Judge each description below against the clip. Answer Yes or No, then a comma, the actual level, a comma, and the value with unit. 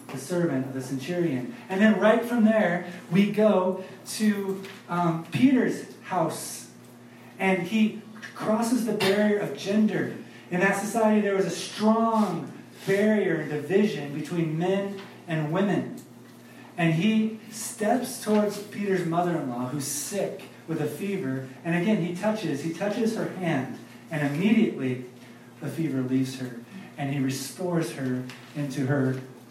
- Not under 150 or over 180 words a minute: No, average, 140 wpm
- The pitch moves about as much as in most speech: No, wide, 6.9 semitones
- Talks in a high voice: No, medium, 175 Hz